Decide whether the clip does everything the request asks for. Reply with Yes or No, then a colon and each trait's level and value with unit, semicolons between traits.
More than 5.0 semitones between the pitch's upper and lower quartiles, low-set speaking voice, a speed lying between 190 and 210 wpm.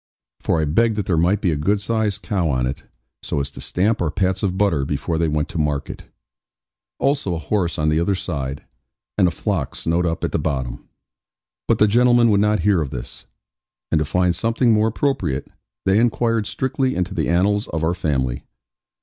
Yes: wide, 5.5 semitones; very low, 90 Hz; average, 200 wpm